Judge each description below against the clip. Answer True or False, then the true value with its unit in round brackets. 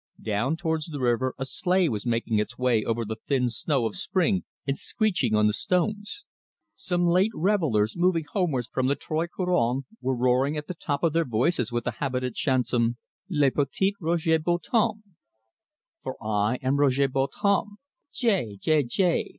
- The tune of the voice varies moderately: False (6.2 semitones)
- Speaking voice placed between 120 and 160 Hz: True (140 Hz)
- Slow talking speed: False (165 wpm)